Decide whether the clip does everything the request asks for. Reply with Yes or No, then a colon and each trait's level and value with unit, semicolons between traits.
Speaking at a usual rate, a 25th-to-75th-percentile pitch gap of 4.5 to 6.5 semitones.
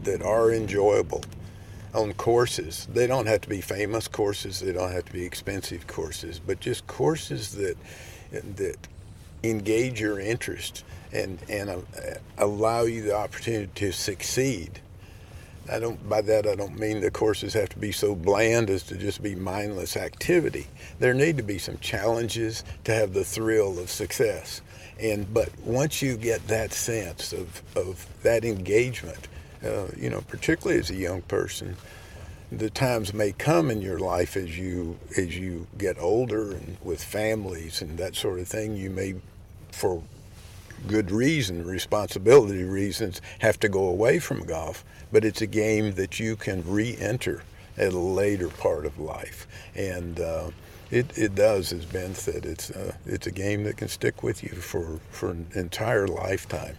No: average, 165 wpm; average, 3.3 semitones